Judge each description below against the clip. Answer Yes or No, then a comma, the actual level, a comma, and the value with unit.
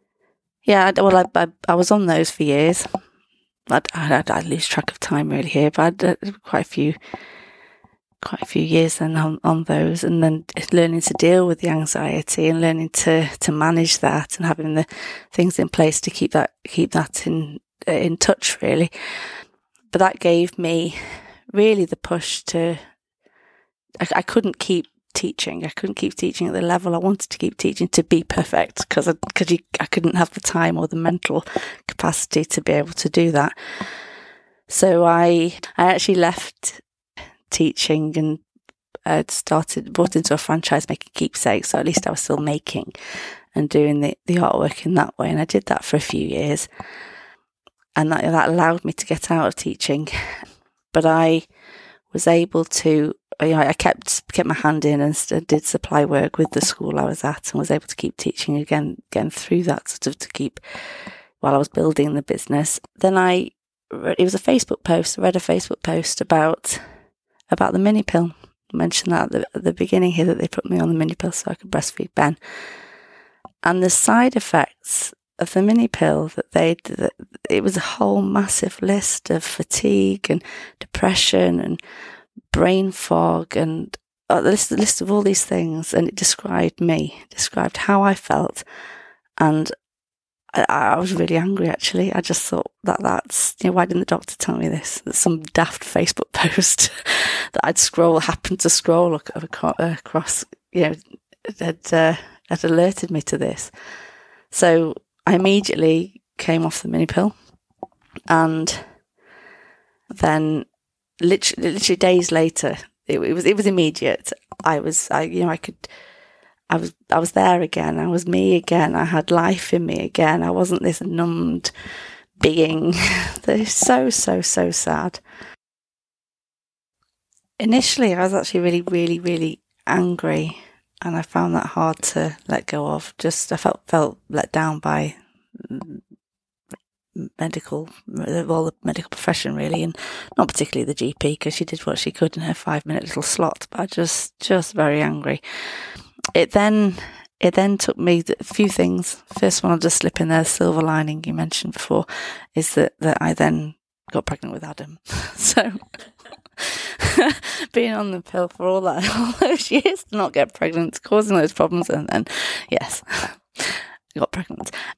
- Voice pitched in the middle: Yes, medium, 165 Hz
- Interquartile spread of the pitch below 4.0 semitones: Yes, average, 3.3 semitones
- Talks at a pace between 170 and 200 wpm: Yes, average, 175 wpm